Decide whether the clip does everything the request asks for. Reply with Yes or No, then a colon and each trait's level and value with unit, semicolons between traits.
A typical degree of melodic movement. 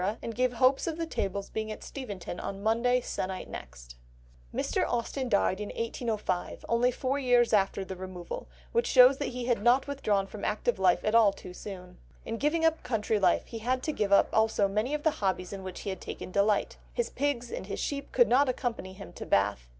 Yes: average, 4.5 semitones